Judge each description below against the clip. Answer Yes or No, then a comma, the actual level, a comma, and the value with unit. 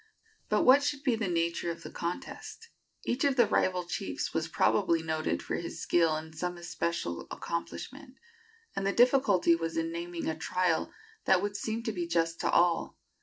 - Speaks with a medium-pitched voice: Yes, medium, 175 Hz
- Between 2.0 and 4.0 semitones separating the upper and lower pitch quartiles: No, average, 4.8 semitones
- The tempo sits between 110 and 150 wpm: No, average, 180 wpm